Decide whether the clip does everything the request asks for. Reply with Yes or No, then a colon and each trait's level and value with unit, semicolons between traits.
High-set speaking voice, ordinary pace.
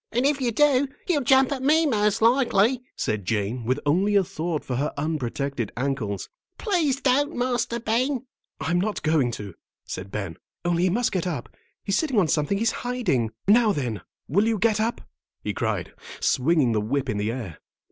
Yes: high, 195 Hz; average, 185 wpm